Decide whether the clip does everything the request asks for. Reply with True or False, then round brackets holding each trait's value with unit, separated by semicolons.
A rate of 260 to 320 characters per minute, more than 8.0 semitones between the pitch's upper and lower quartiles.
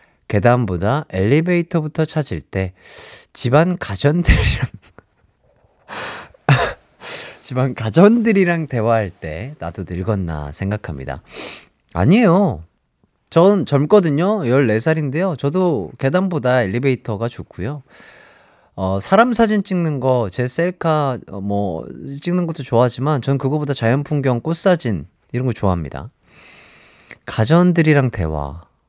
False (245 characters per minute; 8.7 semitones)